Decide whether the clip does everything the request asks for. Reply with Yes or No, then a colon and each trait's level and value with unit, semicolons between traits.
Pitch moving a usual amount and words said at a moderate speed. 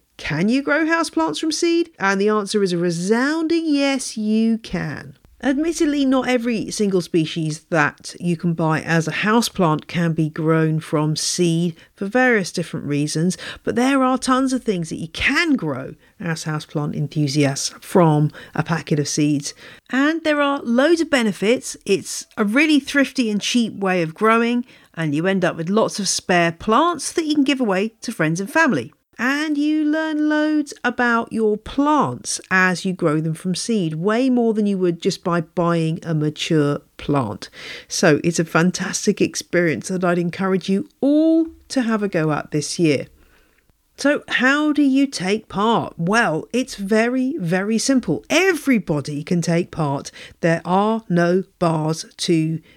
No: wide, 7.7 semitones; average, 170 wpm